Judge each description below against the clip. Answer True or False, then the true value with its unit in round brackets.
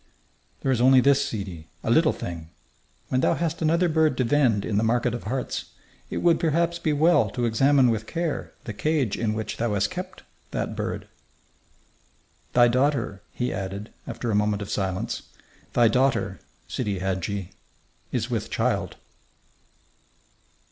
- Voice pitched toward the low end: True (120 Hz)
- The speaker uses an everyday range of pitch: False (5.9 semitones)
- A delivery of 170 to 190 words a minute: False (155 wpm)